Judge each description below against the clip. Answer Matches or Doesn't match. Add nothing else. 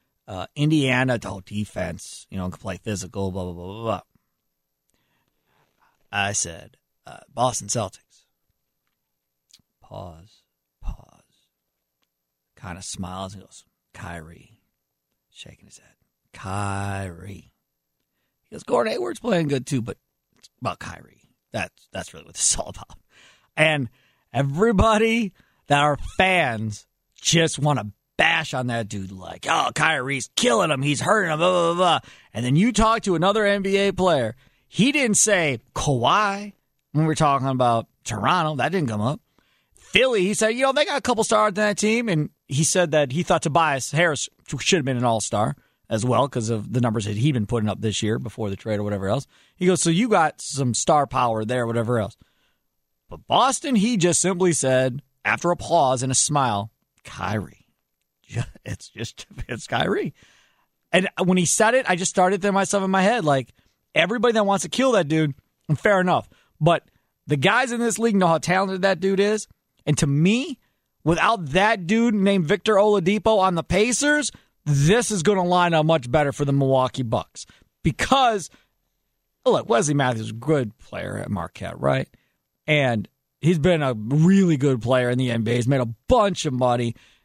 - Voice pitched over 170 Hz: Doesn't match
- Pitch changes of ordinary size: Doesn't match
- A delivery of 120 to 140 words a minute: Doesn't match